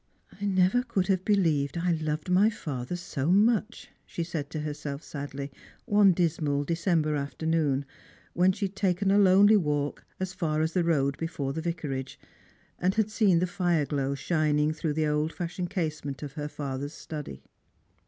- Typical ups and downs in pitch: Yes, average, 4.1 semitones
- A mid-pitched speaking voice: Yes, medium, 165 Hz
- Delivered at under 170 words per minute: No, average, 175 wpm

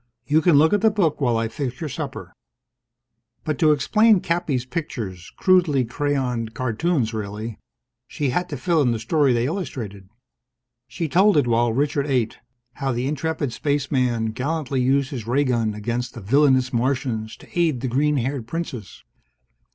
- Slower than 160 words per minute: No, average, 165 wpm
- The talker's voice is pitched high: No, low, 130 Hz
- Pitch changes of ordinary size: Yes, average, 4.5 semitones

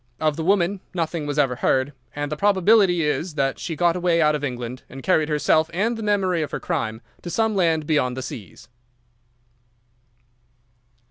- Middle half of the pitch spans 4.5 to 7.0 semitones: No, average, 3.8 semitones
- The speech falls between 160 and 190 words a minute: Yes, average, 180 wpm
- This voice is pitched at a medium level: Yes, medium, 160 Hz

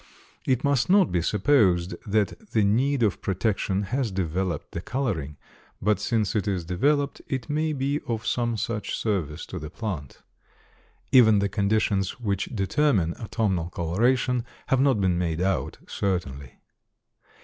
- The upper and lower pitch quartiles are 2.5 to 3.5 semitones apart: No, wide, 5.6 semitones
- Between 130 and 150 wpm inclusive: Yes, average, 145 wpm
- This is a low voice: Yes, low, 105 Hz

